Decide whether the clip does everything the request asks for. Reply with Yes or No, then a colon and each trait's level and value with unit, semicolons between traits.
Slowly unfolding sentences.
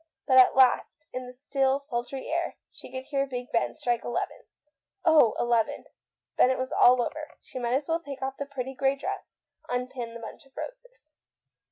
No: average, 190 wpm